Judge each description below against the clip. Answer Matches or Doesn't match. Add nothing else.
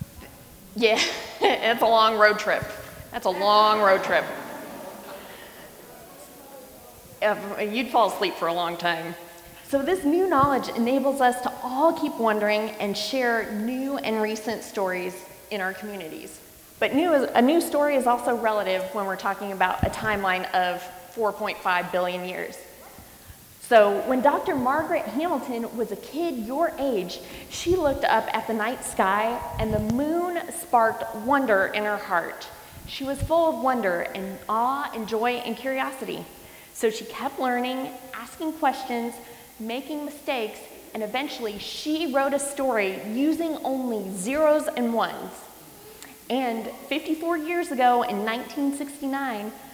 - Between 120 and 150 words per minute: Matches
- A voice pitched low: Doesn't match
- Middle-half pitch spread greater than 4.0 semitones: Matches